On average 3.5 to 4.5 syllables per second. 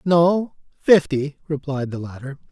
Yes: 4.0 syllables/s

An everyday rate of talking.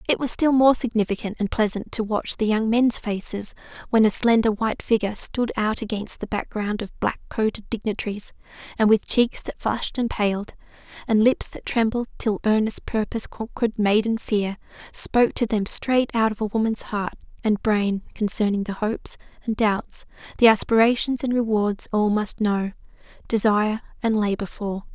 Yes: average, 170 wpm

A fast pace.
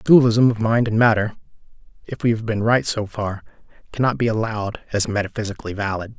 No: average, 185 wpm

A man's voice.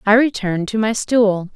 No: female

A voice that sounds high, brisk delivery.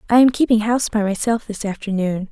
Yes: high, 215 Hz; fast, 210 wpm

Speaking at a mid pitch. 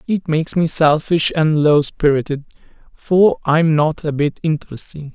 Yes: medium, 155 Hz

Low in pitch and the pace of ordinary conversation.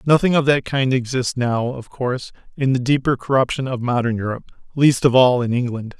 Yes: low, 130 Hz; average, 190 wpm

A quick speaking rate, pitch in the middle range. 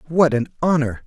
No: average, 170 wpm; medium, 145 Hz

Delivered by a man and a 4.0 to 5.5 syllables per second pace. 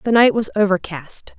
No: female; 5.1 syllables/s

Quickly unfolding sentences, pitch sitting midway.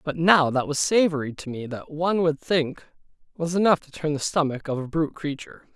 Yes: fast, 220 wpm; medium, 155 Hz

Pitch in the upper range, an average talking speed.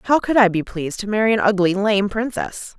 No: high, 210 Hz; fast, 235 wpm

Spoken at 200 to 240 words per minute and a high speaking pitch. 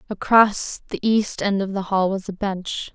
Yes: fast, 205 wpm; high, 195 Hz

